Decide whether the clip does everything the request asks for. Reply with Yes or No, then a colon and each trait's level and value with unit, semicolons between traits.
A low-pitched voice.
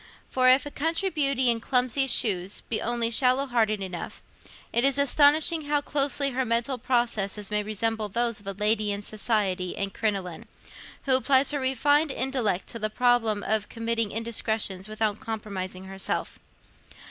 No: high, 230 Hz